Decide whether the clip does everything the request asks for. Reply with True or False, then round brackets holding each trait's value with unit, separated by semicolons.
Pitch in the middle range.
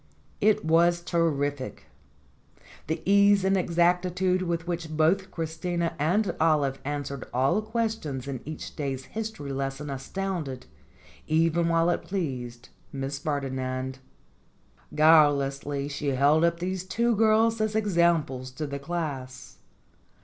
True (160 Hz)